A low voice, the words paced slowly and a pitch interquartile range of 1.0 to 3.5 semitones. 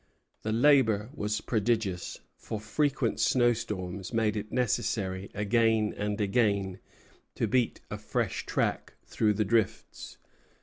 Yes: low, 110 Hz; slow, 120 wpm; narrow, 2.4 semitones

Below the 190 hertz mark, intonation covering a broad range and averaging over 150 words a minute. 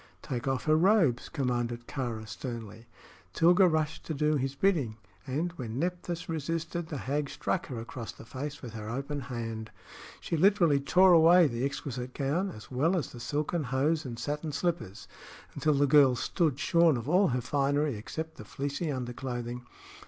No: medium, 140 Hz; average, 4.8 semitones; average, 170 wpm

